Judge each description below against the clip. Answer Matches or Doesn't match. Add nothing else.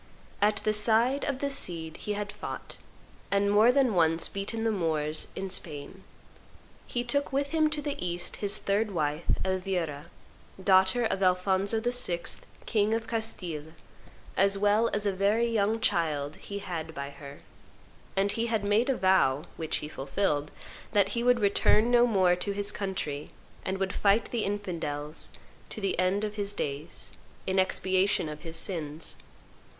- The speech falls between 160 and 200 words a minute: Matches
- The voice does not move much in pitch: Doesn't match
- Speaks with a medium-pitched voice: Doesn't match